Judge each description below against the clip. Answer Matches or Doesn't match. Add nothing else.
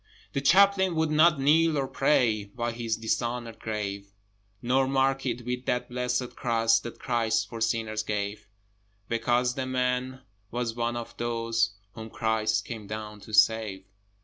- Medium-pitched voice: Doesn't match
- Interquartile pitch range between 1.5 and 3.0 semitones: Matches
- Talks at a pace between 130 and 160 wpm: Matches